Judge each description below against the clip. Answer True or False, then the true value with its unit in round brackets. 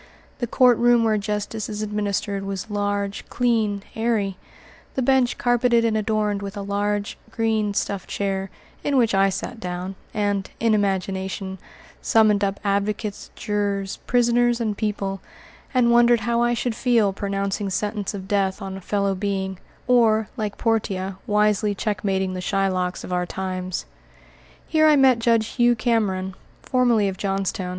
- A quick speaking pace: False (150 wpm)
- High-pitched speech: True (205 Hz)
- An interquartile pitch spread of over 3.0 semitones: False (2.7 semitones)